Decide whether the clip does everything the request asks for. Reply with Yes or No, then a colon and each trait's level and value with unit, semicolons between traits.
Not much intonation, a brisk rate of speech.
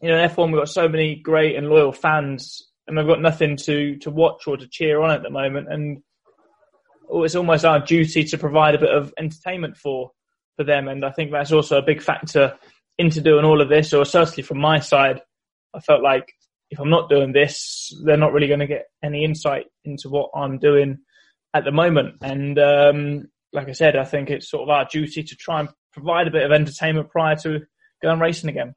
Yes: narrow, 1.8 semitones; fast, 220 wpm